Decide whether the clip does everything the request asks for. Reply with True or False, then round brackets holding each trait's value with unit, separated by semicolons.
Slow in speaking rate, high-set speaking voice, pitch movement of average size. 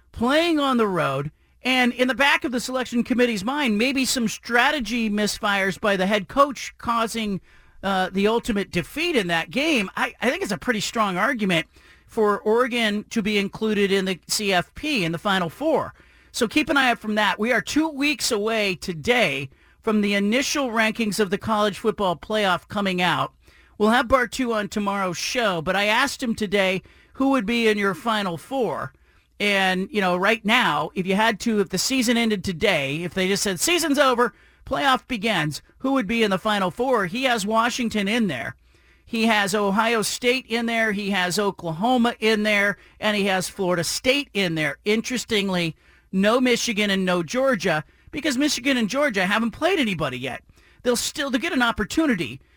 False (185 wpm; 215 Hz; 4.1 semitones)